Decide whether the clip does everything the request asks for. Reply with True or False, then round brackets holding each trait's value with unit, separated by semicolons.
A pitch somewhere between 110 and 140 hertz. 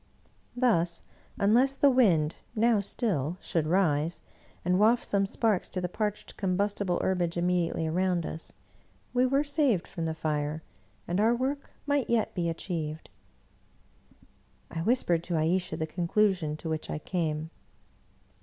False (180 Hz)